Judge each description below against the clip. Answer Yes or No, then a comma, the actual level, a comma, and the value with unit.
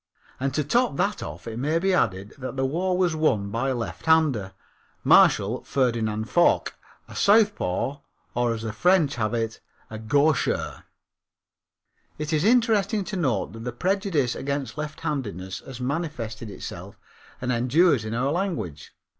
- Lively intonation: Yes, wide, 6.8 semitones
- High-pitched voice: No, low, 135 Hz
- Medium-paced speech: Yes, average, 145 wpm